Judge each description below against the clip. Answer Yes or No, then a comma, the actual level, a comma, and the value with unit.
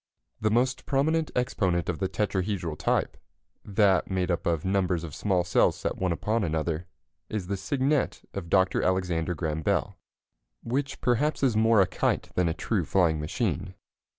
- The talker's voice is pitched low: Yes, very low, 95 Hz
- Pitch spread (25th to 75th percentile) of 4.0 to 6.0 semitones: Yes, average, 4.5 semitones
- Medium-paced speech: Yes, average, 165 wpm